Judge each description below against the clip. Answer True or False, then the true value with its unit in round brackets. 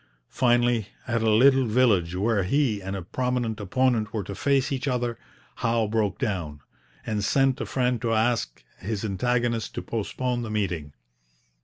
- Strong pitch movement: False (3.4 semitones)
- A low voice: True (115 Hz)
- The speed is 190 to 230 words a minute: False (160 wpm)